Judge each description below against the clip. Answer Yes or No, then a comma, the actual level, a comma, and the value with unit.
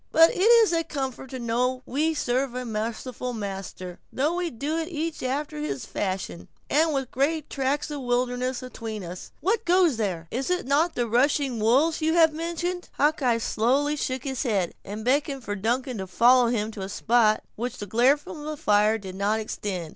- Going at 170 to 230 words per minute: Yes, average, 200 wpm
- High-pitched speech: Yes, very high, 255 Hz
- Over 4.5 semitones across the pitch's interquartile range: Yes, wide, 5.5 semitones